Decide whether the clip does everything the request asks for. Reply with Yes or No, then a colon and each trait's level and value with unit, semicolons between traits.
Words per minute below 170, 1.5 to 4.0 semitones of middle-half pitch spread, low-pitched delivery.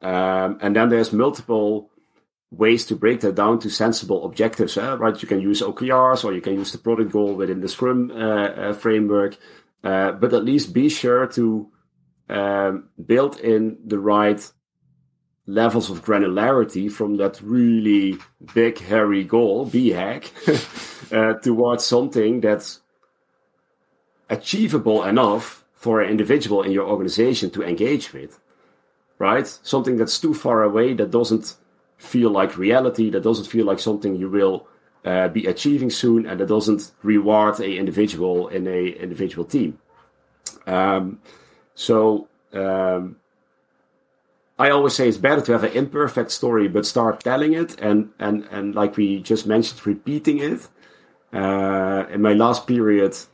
Yes: average, 150 wpm; average, 2.9 semitones; low, 105 Hz